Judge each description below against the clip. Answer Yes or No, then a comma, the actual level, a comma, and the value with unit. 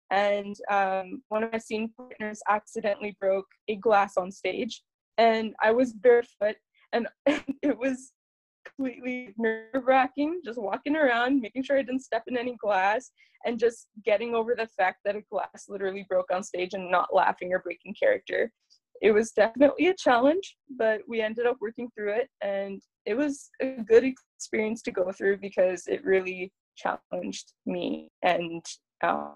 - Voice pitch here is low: No, high, 220 Hz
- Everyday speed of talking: Yes, average, 165 wpm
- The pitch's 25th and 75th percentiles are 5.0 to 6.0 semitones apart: No, average, 4.3 semitones